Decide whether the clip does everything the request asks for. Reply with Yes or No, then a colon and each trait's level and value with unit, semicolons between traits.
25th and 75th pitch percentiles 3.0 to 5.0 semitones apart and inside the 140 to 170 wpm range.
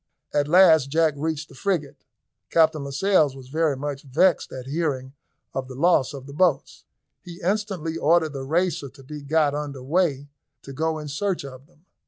No: average, 3.3 semitones; average, 180 wpm